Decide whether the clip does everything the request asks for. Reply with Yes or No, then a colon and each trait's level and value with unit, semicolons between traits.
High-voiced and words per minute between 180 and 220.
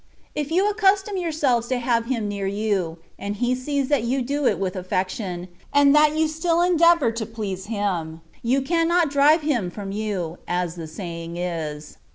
Yes: high, 235 Hz; average, 185 wpm